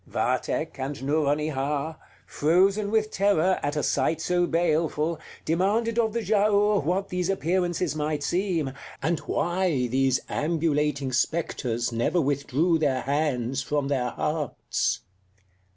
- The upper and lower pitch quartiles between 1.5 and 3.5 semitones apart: No, average, 4.3 semitones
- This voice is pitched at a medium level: Yes, medium, 155 Hz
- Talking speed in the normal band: No, slow, 120 wpm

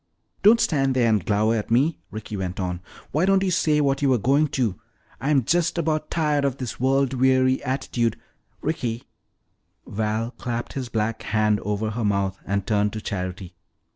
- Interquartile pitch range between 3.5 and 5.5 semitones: Yes, average, 4.7 semitones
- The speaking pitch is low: Yes, low, 120 Hz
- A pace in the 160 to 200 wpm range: Yes, average, 180 wpm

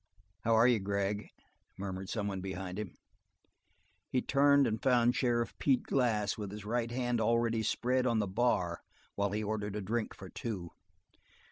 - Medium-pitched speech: No, low, 110 Hz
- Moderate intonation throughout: Yes, average, 3.2 semitones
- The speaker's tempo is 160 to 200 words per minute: Yes, average, 165 wpm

